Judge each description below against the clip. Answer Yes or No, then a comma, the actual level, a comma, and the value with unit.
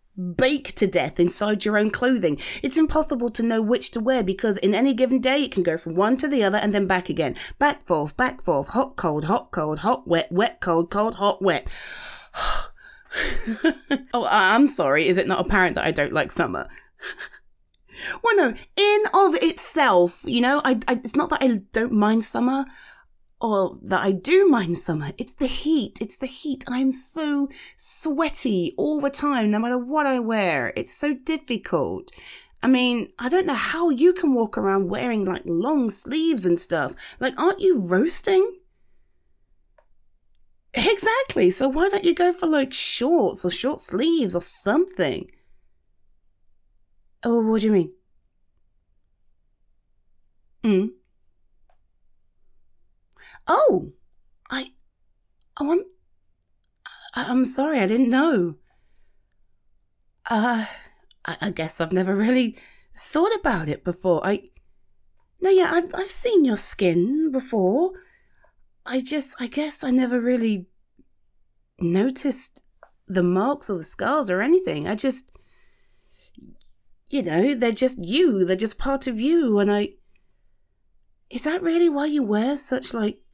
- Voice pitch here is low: No, high, 240 Hz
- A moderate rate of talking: Yes, average, 150 wpm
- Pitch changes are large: Yes, wide, 8.3 semitones